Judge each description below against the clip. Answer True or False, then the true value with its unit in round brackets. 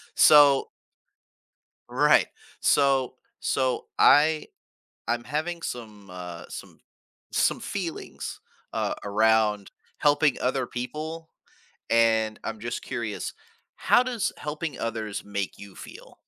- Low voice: True (125 Hz)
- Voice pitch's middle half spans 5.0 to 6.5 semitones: True (5.5 semitones)